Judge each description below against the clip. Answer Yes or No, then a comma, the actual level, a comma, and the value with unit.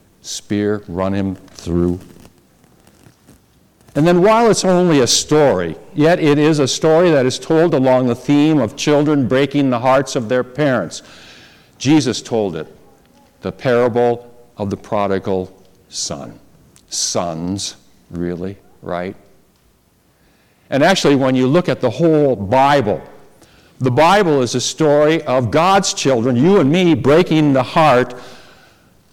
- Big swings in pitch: Yes, wide, 6.7 semitones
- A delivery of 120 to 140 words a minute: Yes, slow, 135 wpm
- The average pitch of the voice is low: Yes, low, 130 Hz